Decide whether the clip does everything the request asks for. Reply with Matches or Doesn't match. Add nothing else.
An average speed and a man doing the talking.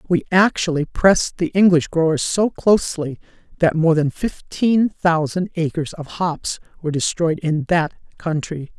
Doesn't match